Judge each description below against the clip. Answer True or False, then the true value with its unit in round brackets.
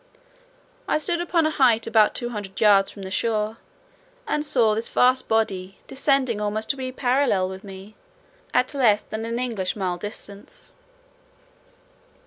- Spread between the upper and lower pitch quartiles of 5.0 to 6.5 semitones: False (4.0 semitones)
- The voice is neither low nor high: False (220 Hz)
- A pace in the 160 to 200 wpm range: False (150 wpm)